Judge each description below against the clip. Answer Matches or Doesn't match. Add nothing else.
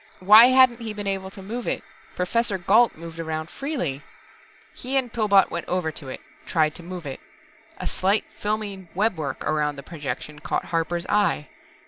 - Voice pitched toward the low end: Doesn't match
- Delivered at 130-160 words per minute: Doesn't match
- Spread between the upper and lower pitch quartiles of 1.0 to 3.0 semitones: Doesn't match